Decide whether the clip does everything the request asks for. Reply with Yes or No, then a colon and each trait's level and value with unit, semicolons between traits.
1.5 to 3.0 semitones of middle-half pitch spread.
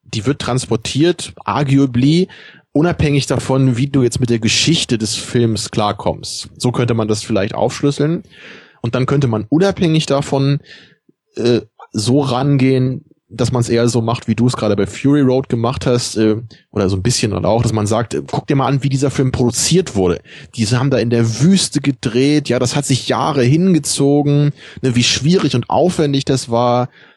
No: average, 3.6 semitones